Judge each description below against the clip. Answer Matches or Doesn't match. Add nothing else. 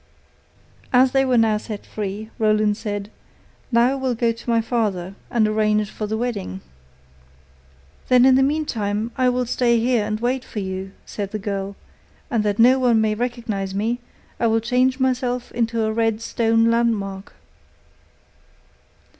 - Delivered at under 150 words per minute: Doesn't match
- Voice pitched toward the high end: Matches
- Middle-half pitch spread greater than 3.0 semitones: Doesn't match